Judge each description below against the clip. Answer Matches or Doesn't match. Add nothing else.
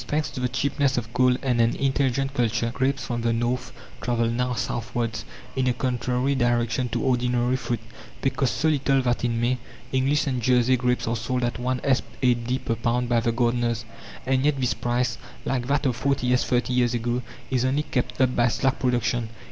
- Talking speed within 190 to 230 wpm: Matches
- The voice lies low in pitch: Matches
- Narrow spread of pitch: Matches